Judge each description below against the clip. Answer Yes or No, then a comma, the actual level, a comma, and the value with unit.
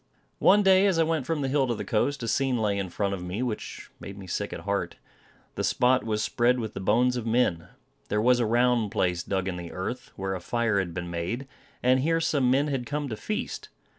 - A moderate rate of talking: No, fast, 240 wpm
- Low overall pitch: Yes, low, 120 Hz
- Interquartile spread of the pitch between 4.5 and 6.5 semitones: Yes, average, 5.2 semitones